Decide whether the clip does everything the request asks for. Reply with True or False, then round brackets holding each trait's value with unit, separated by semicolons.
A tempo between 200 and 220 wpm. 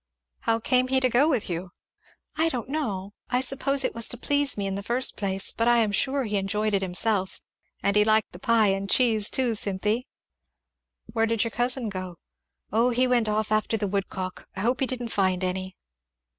True (205 wpm)